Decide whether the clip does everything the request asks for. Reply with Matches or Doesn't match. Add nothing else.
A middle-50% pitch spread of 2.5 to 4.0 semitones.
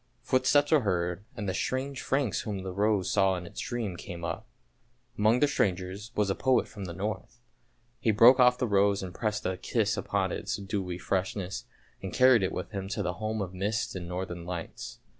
Matches